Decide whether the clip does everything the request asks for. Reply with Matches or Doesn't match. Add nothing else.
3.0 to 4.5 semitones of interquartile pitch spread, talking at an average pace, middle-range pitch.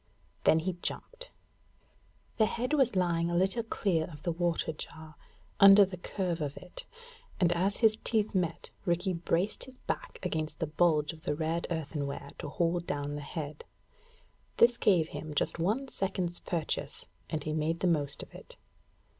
Matches